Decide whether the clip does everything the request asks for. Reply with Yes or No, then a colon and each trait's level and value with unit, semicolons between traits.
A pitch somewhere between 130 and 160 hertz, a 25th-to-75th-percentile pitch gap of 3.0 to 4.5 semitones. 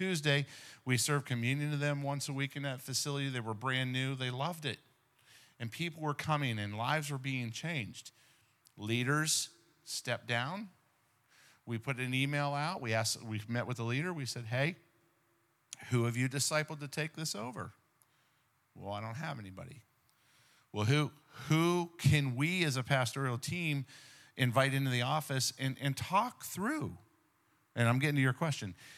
Yes: low, 135 Hz; average, 3.4 semitones